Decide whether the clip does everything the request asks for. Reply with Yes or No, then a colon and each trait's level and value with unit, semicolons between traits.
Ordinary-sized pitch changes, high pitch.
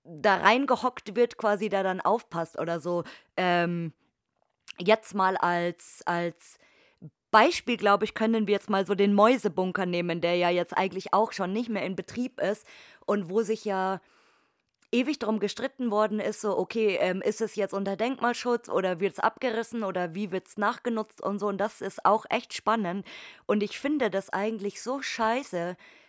Yes: average, 3.1 semitones; high, 205 Hz